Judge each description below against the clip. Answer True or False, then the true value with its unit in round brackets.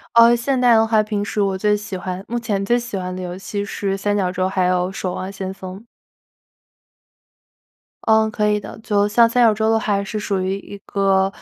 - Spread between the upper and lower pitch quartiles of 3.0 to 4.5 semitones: False (2.5 semitones)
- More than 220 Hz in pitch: False (205 Hz)